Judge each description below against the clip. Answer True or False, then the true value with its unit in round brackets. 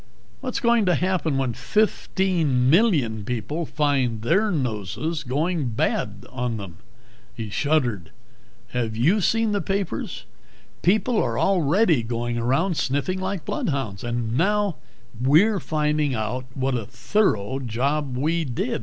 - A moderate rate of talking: False (130 wpm)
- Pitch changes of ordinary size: False (7.2 semitones)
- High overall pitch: False (140 Hz)